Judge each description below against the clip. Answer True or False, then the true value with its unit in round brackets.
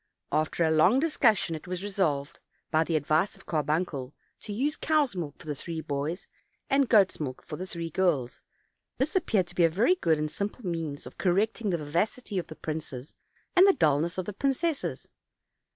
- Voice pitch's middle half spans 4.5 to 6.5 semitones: True (5.2 semitones)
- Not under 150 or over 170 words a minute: False (190 wpm)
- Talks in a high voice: False (175 Hz)